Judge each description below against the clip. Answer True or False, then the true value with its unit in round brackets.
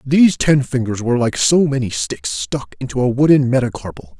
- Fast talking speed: False (185 wpm)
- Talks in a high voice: False (130 Hz)